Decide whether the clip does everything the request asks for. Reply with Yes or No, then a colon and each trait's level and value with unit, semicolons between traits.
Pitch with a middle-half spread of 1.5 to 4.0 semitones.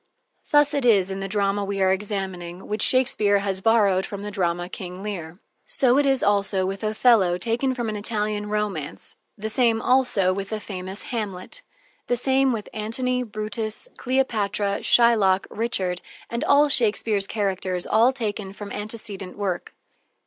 Yes: average, 3.2 semitones